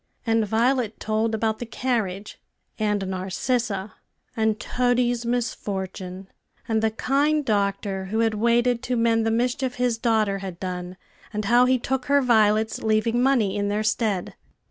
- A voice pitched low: No, high, 225 Hz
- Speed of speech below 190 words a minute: Yes, average, 150 wpm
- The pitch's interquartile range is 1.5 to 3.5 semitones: Yes, average, 3.0 semitones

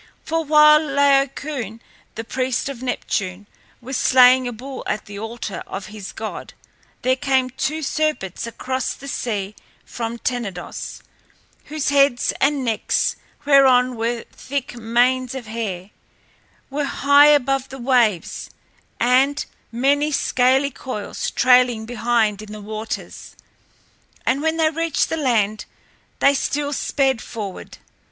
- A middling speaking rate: No, slow, 130 wpm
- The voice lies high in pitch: Yes, very high, 255 Hz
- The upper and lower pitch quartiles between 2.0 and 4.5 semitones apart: Yes, average, 3.7 semitones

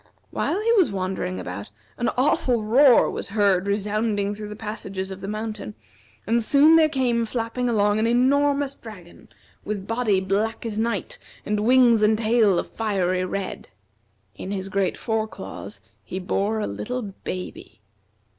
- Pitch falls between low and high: No, high, 215 Hz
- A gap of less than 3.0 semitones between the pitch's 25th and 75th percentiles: No, average, 3.4 semitones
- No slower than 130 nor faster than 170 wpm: Yes, average, 155 wpm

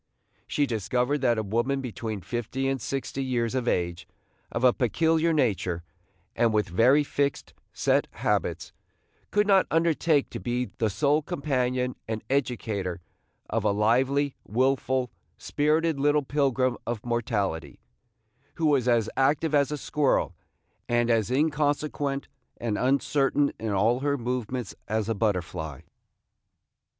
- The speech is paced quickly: No, slow, 135 wpm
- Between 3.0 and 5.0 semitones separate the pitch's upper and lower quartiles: Yes, average, 4.2 semitones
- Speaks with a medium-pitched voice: No, low, 125 Hz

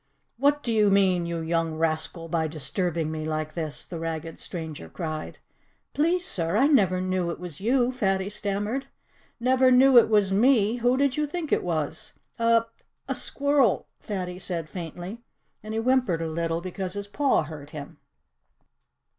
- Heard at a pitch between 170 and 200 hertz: Yes, high, 190 Hz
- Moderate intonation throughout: No, wide, 6.4 semitones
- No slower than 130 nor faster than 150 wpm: No, average, 165 wpm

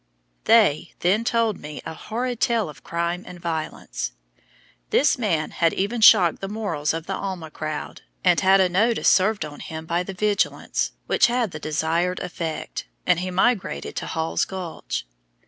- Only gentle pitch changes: No, average, 4.7 semitones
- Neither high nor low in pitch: Yes, medium, 180 Hz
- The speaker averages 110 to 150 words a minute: No, average, 165 wpm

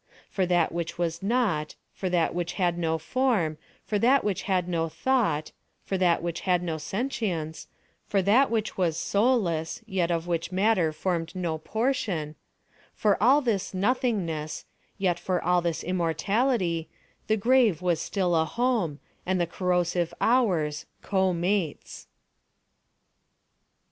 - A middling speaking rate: No, slow, 130 wpm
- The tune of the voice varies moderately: Yes, average, 4.1 semitones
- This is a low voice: No, medium, 180 Hz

